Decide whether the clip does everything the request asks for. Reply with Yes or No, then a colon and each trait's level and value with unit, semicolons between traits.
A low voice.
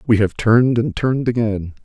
Yes: low, 115 Hz